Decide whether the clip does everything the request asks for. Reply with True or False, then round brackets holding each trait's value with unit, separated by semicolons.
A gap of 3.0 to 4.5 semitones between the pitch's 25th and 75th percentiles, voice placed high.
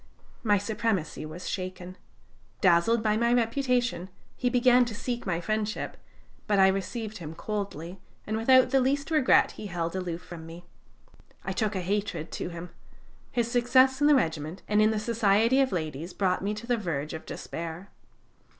False (5.1 semitones; 205 Hz)